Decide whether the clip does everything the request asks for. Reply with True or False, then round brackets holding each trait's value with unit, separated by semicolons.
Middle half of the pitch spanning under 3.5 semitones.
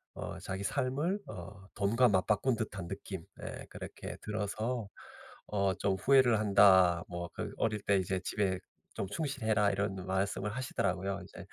True (2.6 semitones)